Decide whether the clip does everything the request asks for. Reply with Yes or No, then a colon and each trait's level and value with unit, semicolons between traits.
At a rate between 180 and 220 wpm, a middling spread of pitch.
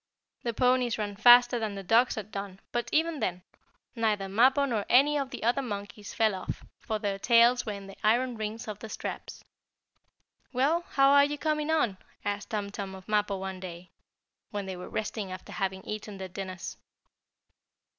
Yes: average, 185 wpm; average, 4.0 semitones